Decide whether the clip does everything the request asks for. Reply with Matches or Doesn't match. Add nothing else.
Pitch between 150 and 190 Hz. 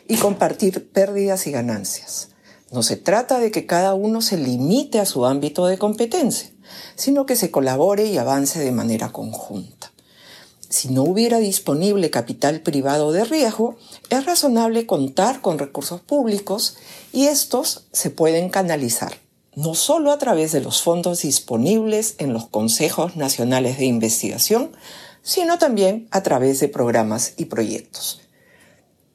Matches